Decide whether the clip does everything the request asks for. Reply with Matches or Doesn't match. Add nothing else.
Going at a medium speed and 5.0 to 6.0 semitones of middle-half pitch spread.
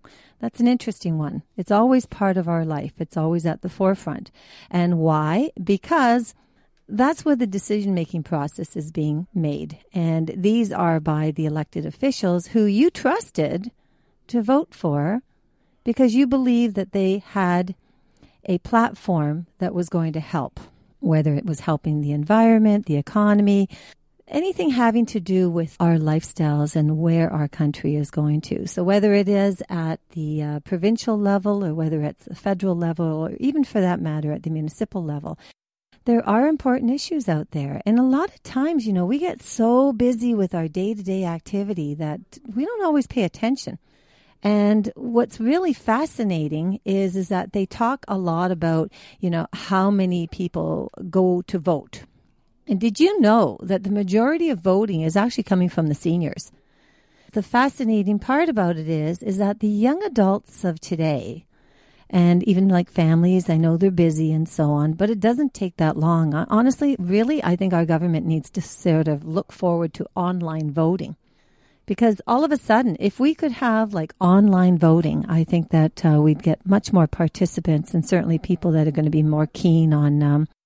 Matches